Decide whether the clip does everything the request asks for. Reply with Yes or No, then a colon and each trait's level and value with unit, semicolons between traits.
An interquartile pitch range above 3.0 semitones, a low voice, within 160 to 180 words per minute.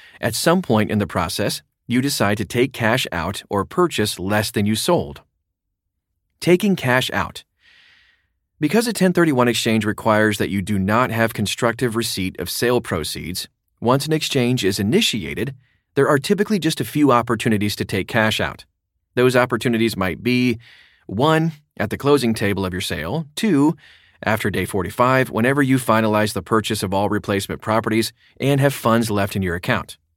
Yes: average, 4.5 semitones; low, 110 Hz; average, 165 wpm